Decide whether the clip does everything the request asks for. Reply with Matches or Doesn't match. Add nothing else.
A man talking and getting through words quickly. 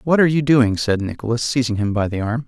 Matches